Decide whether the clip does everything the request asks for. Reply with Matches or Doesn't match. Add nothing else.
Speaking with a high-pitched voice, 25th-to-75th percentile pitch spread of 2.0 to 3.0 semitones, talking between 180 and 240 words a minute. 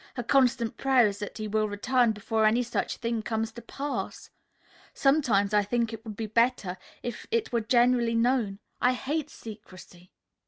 Doesn't match